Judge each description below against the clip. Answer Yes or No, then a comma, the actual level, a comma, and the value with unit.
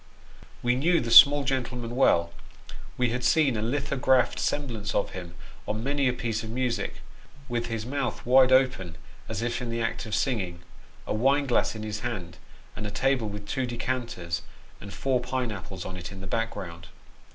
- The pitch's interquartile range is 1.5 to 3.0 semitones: No, average, 3.8 semitones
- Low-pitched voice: Yes, low, 120 Hz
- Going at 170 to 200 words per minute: Yes, average, 185 wpm